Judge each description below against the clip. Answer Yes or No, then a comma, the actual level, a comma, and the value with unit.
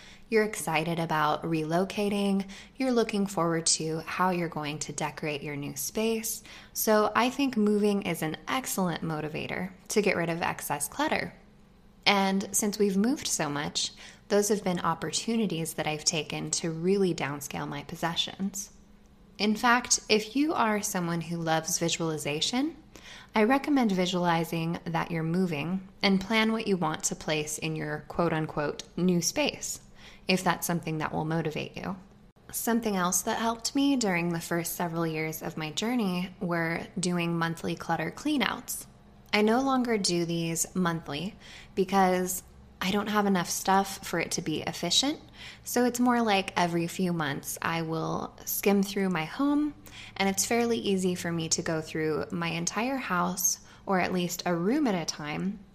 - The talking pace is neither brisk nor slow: Yes, average, 165 wpm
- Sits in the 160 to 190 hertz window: Yes, medium, 185 Hz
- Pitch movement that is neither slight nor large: Yes, average, 4.0 semitones